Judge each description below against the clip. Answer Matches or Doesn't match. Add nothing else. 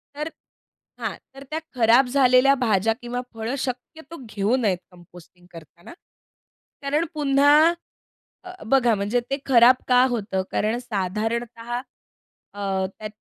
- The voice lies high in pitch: Matches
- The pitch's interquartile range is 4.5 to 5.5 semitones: Matches